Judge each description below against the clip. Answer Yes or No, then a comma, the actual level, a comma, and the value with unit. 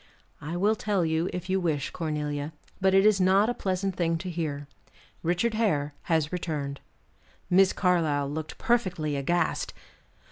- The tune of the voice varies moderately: Yes, average, 3.9 semitones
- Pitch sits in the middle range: Yes, medium, 175 Hz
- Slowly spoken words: No, average, 150 wpm